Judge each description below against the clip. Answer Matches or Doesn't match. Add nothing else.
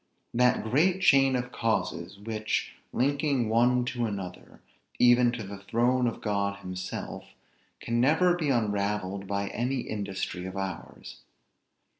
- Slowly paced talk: Matches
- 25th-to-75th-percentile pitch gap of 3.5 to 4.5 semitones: Matches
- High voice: Doesn't match